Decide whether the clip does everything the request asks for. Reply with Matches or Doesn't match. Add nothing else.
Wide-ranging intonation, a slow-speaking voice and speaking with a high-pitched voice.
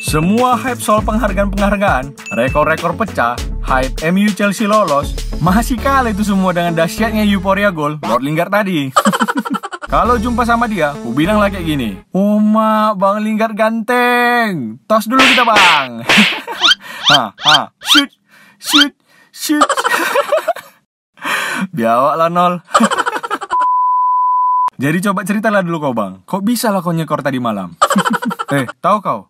Doesn't match